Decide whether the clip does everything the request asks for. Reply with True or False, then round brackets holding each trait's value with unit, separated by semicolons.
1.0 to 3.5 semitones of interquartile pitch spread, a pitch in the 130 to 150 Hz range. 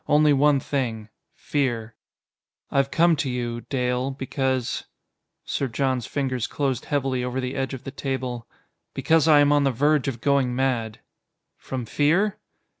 True (2.4 semitones; 135 Hz)